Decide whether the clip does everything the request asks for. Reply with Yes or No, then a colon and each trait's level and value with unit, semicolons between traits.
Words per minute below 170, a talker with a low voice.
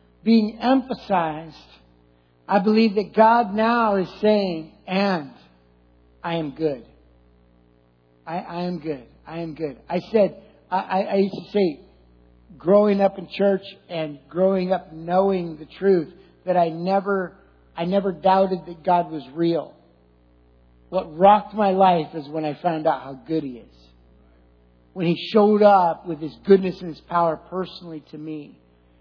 No: average, 150 wpm; medium, 170 Hz